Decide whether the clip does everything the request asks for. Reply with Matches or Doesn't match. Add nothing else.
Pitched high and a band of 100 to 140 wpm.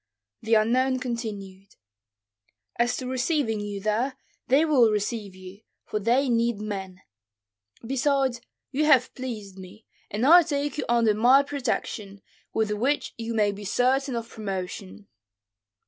Matches